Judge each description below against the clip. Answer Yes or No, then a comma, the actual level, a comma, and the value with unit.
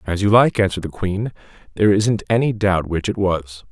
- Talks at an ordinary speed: No, fast, 210 wpm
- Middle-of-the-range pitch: No, low, 100 Hz